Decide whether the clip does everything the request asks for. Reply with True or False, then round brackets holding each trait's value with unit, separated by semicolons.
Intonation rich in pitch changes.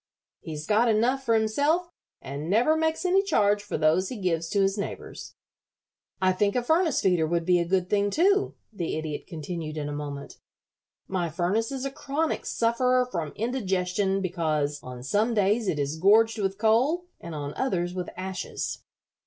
True (6.0 semitones)